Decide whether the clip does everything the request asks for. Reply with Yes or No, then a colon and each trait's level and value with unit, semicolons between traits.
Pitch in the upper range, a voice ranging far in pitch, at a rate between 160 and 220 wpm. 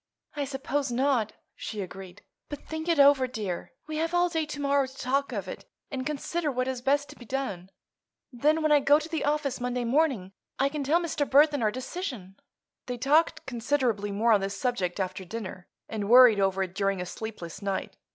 Yes: very high, 255 Hz; wide, 5.9 semitones; average, 200 wpm